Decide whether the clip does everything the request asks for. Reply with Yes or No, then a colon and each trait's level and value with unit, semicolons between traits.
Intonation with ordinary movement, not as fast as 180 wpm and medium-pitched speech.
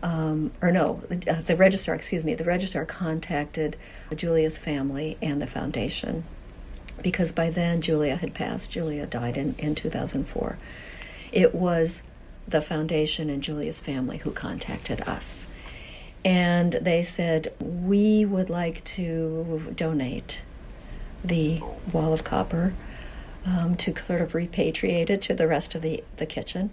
No: narrow, 2.2 semitones; average, 140 wpm; medium, 165 Hz